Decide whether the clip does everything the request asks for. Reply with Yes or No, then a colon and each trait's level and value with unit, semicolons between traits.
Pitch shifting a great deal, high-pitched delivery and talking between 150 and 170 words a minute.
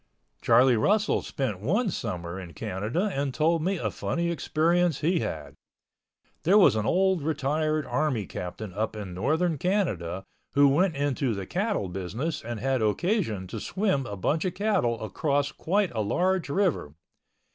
No: wide, 8.6 semitones; medium, 140 Hz; average, 155 wpm